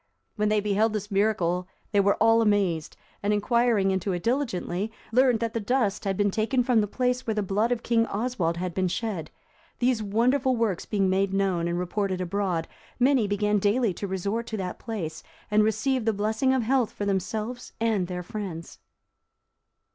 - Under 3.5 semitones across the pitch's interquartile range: Yes, average, 3.1 semitones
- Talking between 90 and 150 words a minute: No, average, 185 wpm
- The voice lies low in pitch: No, high, 210 Hz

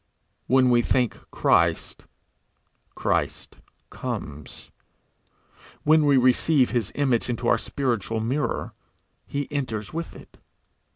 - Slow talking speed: Yes, slow, 105 wpm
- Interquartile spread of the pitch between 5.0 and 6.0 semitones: No, average, 3.7 semitones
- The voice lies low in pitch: Yes, low, 125 Hz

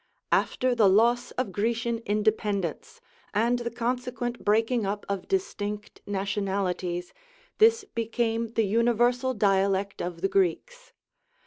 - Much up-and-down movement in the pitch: No, average, 3.4 semitones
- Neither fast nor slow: No, slow, 120 wpm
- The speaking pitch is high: Yes, high, 225 Hz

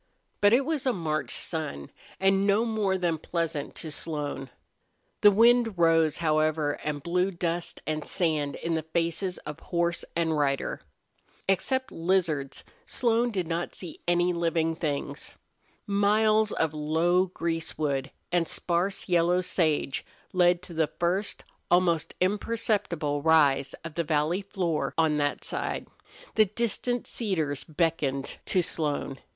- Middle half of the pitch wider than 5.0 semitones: No, average, 3.7 semitones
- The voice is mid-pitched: Yes, medium, 170 Hz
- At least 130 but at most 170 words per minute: Yes, slow, 135 wpm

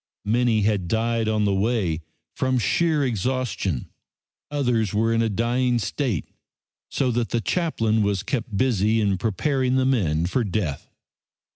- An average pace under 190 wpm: Yes, average, 145 wpm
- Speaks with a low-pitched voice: Yes, low, 115 Hz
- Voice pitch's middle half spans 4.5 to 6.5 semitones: No, average, 3.8 semitones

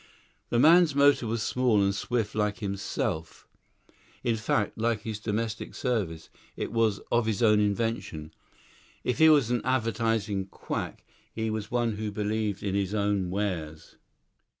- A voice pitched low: Yes, low, 110 Hz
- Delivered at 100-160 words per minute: Yes, average, 150 wpm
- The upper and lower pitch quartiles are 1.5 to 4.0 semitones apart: Yes, narrow, 2.6 semitones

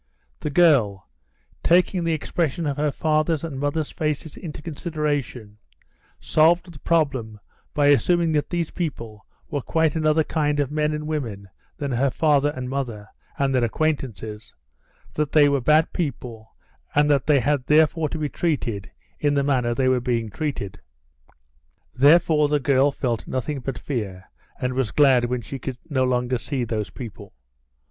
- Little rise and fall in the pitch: No, average, 3.7 semitones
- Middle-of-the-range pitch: Yes, medium, 145 Hz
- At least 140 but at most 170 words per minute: Yes, average, 160 wpm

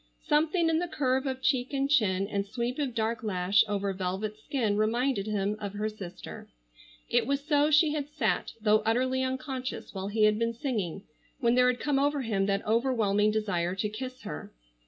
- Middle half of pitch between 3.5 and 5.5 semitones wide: Yes, average, 4.5 semitones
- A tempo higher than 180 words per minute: Yes, average, 190 wpm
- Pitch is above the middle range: Yes, high, 230 Hz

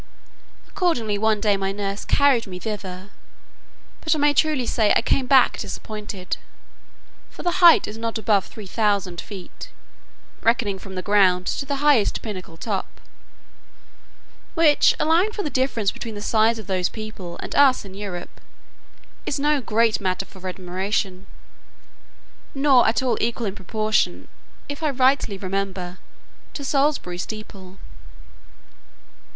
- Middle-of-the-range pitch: No, high, 215 Hz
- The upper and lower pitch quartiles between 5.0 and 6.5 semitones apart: Yes, wide, 5.4 semitones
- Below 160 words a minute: Yes, average, 140 wpm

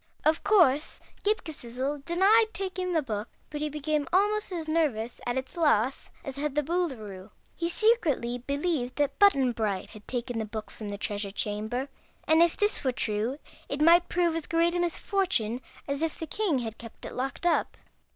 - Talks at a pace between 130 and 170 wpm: No, average, 185 wpm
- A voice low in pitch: No, very high, 290 Hz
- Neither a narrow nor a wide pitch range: No, wide, 6.2 semitones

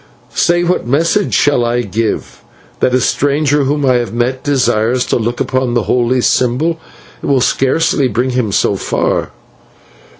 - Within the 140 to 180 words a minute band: Yes, average, 160 wpm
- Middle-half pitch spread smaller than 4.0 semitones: Yes, average, 3.1 semitones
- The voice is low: Yes, low, 130 Hz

